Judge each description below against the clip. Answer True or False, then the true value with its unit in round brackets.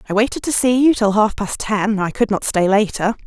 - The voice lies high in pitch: True (215 Hz)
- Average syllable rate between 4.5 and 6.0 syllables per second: True (5.3 syllables/s)